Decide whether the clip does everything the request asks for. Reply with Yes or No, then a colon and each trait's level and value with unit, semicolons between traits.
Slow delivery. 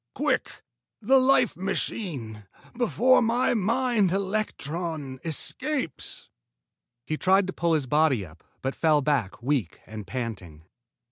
Yes: slow, 120 wpm